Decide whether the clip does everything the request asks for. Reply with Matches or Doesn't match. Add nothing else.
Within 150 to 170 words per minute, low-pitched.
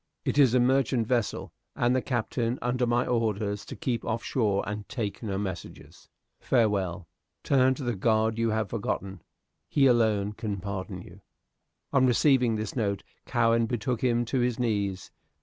Matches